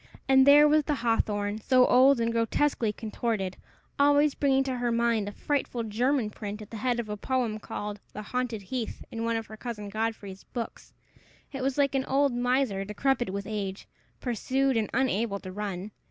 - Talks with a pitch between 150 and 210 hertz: No, high, 230 Hz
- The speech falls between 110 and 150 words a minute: No, average, 185 wpm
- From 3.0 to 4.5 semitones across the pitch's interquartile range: Yes, average, 3.9 semitones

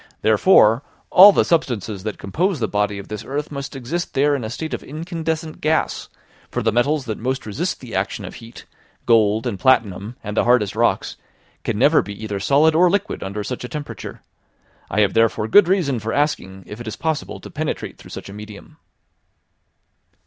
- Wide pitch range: Yes, wide, 6.3 semitones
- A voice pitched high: No, low, 120 Hz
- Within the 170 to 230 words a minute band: Yes, average, 190 wpm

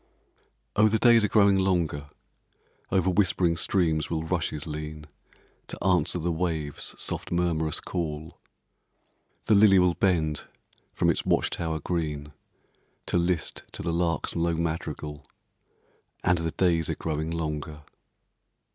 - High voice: No, very low, 85 Hz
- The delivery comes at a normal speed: No, slow, 130 wpm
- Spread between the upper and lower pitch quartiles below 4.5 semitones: Yes, narrow, 2.6 semitones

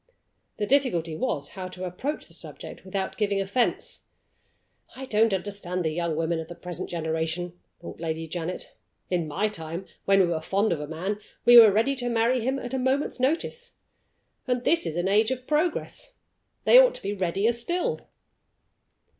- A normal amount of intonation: No, wide, 6.5 semitones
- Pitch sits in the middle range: No, high, 195 Hz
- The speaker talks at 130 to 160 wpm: No, average, 180 wpm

